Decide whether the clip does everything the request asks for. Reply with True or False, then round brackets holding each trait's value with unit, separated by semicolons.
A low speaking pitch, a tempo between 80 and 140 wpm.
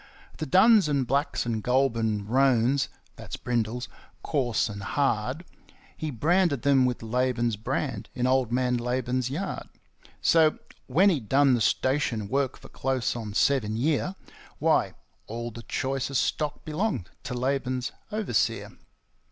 True (130 Hz; 135 wpm)